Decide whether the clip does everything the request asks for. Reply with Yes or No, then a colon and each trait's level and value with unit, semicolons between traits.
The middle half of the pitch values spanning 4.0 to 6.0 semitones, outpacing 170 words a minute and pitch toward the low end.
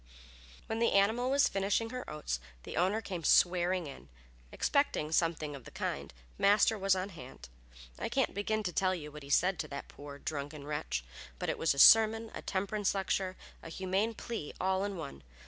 No: average, 5.3 semitones; average, 195 wpm; medium, 185 Hz